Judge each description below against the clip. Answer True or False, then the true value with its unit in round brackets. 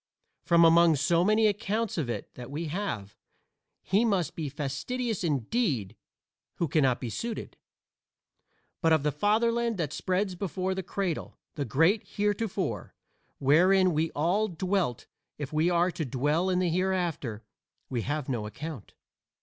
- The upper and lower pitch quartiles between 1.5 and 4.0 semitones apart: False (5.2 semitones)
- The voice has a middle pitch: True (170 Hz)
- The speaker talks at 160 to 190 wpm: False (145 wpm)